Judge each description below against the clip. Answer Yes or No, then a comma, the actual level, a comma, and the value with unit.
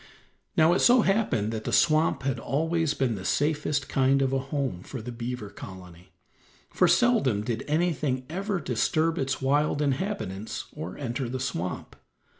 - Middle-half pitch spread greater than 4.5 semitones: Yes, average, 5.2 semitones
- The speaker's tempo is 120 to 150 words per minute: No, average, 160 wpm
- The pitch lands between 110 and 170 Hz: Yes, low, 135 Hz